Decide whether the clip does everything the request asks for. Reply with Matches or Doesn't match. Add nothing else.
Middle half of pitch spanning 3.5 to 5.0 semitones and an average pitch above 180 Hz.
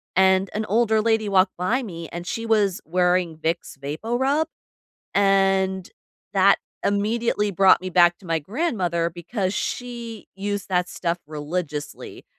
Matches